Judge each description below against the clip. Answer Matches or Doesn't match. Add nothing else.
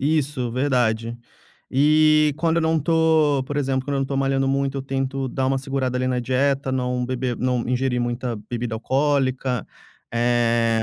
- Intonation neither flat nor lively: Doesn't match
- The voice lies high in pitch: Doesn't match